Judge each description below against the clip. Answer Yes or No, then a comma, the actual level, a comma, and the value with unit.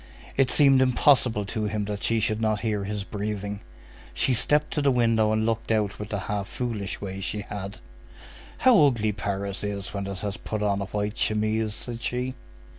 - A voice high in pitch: No, low, 105 Hz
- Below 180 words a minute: No, average, 190 wpm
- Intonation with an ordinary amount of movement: No, narrow, 2.3 semitones